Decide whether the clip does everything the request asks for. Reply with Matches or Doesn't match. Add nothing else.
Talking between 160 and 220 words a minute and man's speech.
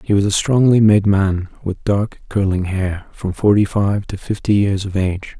Matches